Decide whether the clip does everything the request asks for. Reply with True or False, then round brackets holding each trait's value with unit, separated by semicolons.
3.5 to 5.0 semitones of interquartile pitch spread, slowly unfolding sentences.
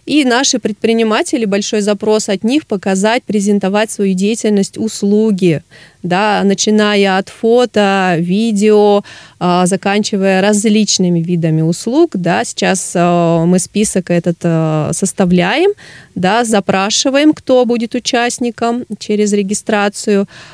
False (3.0 semitones; 100 wpm)